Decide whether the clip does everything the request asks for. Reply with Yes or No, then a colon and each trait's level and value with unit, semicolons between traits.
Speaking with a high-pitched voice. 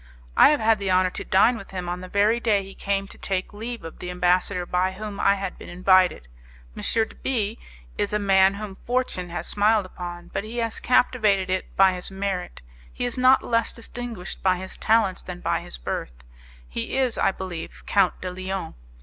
Yes: high, 195 Hz